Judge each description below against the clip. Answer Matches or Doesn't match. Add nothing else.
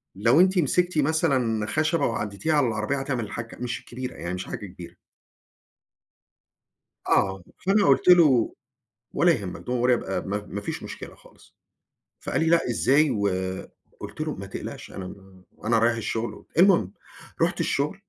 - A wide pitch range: Matches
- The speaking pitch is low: Matches